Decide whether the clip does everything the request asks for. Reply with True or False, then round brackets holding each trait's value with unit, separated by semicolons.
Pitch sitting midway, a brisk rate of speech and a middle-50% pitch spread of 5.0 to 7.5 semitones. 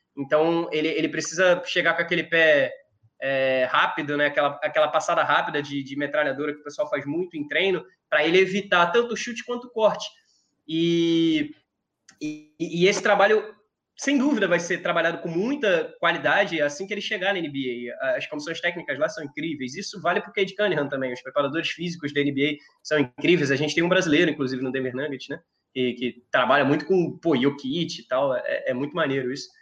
True (165 Hz; 195 wpm; 5.5 semitones)